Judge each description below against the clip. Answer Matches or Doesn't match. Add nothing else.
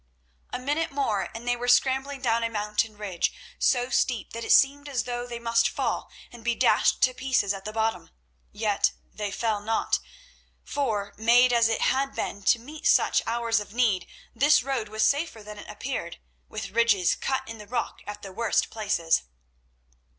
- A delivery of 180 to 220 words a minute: Matches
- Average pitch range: Matches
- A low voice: Doesn't match